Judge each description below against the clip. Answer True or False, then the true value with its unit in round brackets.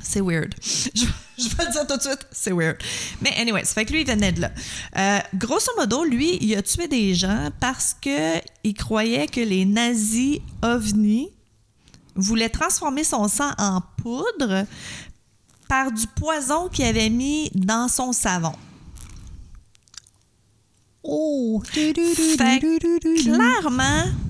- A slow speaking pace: True (140 wpm)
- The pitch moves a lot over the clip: True (7.0 semitones)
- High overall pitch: True (230 Hz)